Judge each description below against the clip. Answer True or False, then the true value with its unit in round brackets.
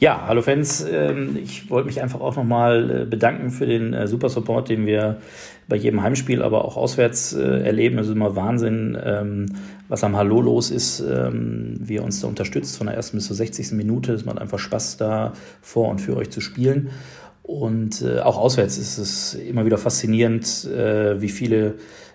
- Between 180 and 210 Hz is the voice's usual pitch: False (110 Hz)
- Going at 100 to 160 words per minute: False (175 wpm)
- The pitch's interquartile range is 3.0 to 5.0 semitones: False (2.4 semitones)